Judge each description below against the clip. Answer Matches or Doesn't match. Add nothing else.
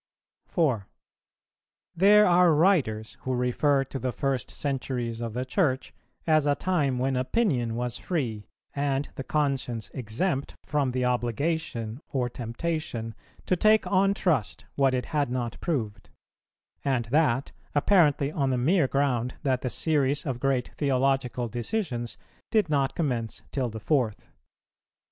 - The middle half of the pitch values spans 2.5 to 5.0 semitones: Matches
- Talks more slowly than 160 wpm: Matches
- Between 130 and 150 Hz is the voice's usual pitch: Matches